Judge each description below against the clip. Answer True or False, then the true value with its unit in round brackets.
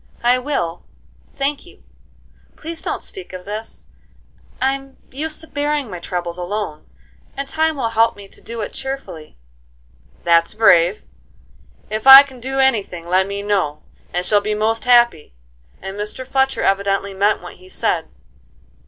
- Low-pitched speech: False (215 Hz)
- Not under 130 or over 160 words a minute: True (155 wpm)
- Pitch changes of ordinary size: False (6.3 semitones)